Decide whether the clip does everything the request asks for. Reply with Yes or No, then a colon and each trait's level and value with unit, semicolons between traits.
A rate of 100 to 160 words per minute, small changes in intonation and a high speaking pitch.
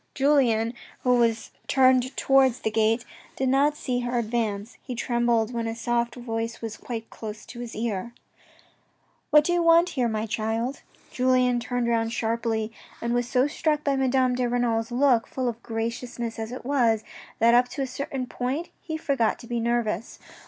No: average, 180 wpm; narrow, 2.3 semitones; high, 240 Hz